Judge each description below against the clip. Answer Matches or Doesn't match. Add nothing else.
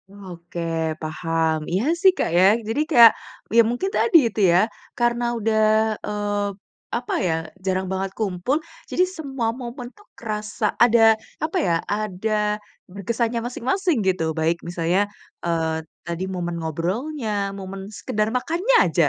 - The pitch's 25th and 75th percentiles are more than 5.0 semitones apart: Matches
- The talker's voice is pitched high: Matches